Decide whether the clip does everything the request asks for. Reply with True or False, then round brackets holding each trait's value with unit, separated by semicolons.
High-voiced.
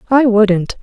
True (220 Hz)